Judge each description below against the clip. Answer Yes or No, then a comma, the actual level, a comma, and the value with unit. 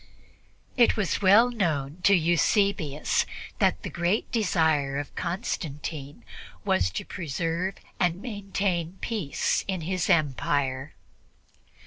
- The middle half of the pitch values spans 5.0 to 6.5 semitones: Yes, average, 5.3 semitones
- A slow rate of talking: Yes, slow, 105 wpm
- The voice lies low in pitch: No, medium, 170 Hz